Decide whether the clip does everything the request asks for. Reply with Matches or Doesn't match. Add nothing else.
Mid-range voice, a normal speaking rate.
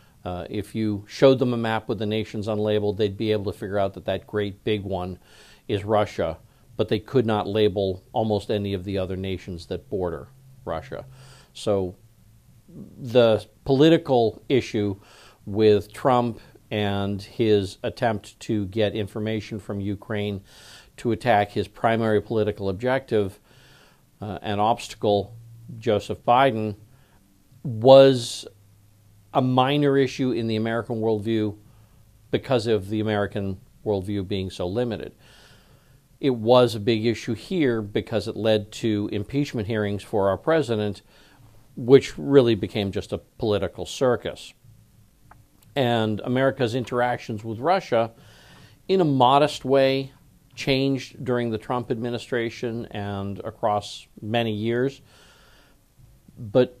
Doesn't match